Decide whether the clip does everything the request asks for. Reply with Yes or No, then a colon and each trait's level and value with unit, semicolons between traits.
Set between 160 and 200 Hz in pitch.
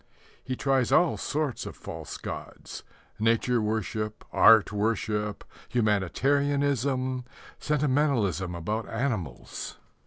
No: low, 115 Hz